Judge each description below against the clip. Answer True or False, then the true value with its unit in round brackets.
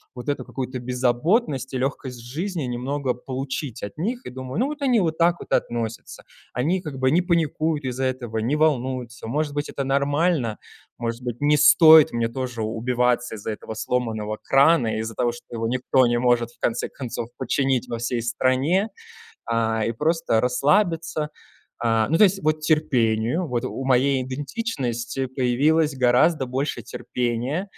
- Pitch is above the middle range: False (130 Hz)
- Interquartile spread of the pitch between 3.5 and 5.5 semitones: True (4.2 semitones)